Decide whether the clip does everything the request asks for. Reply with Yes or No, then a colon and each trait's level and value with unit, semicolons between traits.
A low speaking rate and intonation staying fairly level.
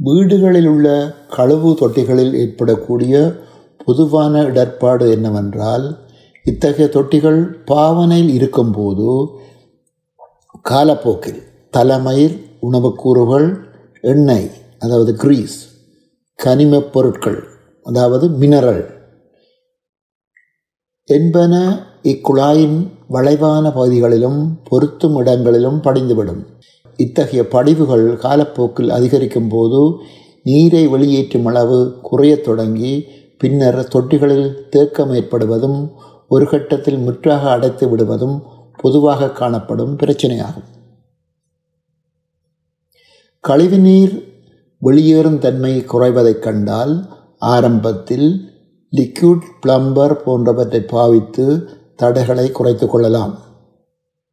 No: slow, 70 wpm; average, 3.8 semitones